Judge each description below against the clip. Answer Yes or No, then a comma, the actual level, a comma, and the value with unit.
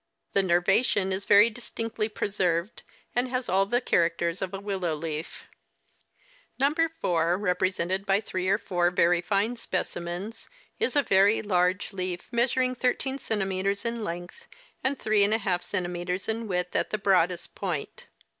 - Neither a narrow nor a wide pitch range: Yes, average, 4.2 semitones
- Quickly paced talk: No, average, 145 wpm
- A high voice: Yes, high, 195 Hz